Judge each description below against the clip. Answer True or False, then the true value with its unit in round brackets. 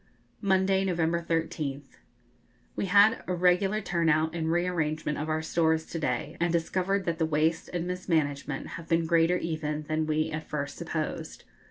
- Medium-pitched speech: True (165 Hz)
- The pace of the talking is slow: False (170 wpm)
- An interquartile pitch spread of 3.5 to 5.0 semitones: False (2.4 semitones)